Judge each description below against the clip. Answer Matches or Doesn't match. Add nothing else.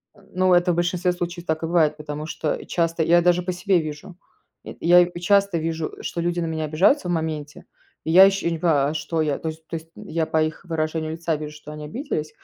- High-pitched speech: Doesn't match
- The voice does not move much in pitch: Matches